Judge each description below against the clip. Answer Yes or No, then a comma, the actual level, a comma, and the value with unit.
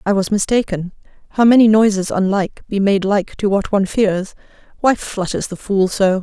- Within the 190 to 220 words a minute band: No, average, 165 wpm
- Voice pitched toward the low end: No, high, 200 Hz